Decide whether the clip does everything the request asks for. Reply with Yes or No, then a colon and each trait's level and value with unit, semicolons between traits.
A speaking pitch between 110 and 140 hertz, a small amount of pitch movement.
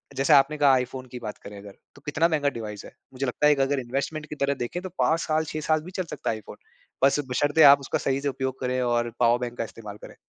No: low, 135 Hz; average, 3.6 semitones